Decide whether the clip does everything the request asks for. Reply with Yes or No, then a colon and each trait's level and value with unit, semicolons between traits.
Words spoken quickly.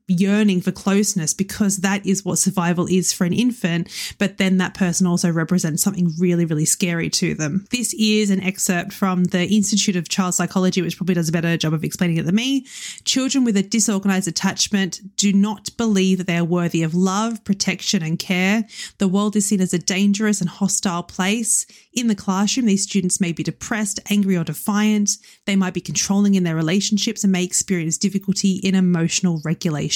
No: average, 195 wpm